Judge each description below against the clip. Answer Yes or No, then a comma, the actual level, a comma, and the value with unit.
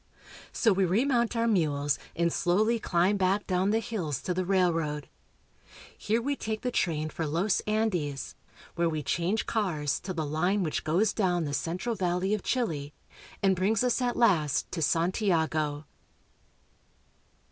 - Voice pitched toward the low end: No, medium, 185 Hz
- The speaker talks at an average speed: Yes, average, 155 wpm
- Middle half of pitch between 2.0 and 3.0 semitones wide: No, average, 5.1 semitones